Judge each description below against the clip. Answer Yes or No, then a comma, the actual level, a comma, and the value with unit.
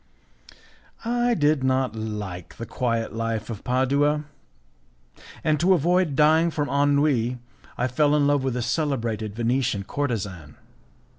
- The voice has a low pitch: Yes, low, 130 Hz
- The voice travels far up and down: No, average, 4.6 semitones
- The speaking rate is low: Yes, slow, 130 wpm